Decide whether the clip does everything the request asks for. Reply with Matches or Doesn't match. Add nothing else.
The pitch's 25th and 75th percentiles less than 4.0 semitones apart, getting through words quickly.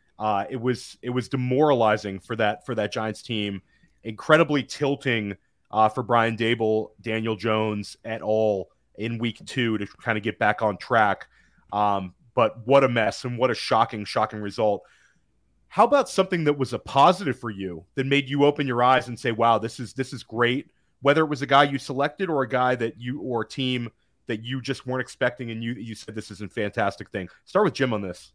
Matches